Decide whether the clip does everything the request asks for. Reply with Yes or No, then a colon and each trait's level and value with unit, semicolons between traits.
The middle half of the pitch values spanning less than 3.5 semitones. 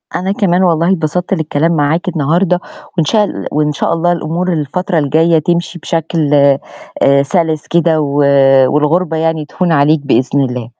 Yes: average, 2.8 semitones